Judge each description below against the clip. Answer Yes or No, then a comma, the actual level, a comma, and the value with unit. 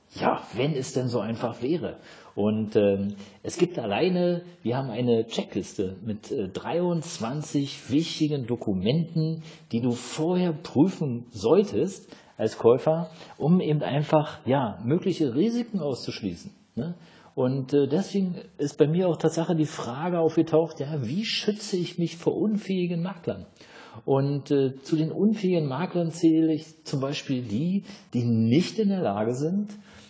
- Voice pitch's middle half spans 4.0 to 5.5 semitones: Yes, average, 5.2 semitones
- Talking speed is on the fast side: No, average, 145 wpm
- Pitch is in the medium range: Yes, medium, 155 Hz